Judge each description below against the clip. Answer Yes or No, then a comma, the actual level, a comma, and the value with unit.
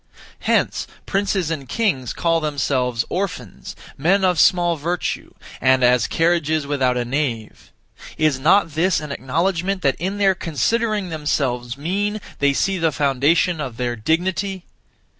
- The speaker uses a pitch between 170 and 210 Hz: No, medium, 160 Hz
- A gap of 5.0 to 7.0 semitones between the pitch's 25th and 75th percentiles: Yes, wide, 5.6 semitones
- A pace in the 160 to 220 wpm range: No, average, 140 wpm